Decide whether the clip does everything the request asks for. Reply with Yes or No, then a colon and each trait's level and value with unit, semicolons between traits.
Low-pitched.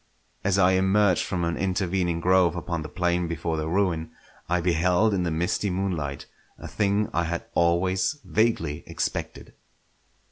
Yes: very low, 90 Hz